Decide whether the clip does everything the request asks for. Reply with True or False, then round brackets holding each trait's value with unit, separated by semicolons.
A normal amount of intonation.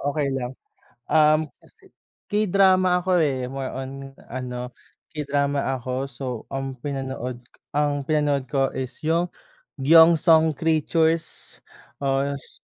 True (3.2 semitones)